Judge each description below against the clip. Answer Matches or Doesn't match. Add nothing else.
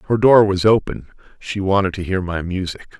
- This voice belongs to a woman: Doesn't match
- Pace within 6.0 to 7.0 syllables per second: Doesn't match